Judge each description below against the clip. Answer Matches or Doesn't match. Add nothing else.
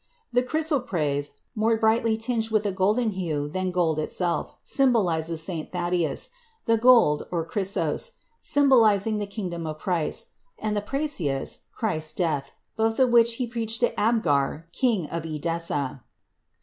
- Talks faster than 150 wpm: Doesn't match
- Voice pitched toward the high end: Matches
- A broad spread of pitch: Matches